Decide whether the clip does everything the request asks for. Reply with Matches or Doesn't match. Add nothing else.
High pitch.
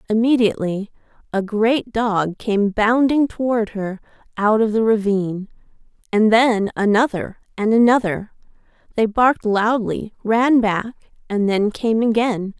Matches